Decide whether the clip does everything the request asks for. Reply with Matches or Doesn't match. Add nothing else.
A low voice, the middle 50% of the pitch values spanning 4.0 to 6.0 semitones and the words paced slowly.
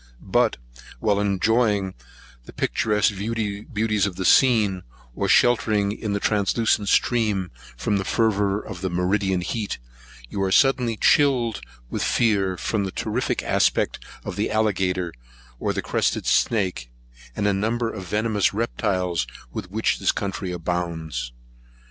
Doesn't match